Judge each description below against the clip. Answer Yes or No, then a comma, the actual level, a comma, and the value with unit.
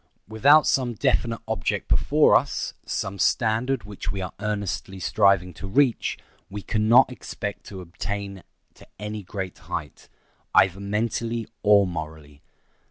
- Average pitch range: Yes, average, 3.1 semitones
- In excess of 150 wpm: No, slow, 135 wpm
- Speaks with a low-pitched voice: Yes, low, 100 Hz